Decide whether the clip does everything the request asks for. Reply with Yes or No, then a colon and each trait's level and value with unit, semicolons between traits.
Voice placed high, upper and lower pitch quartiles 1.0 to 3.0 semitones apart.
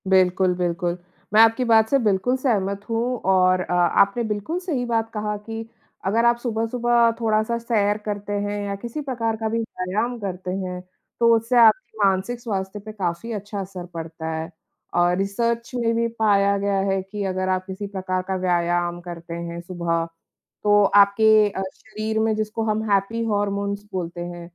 No: high, 205 Hz; average, 3.4 semitones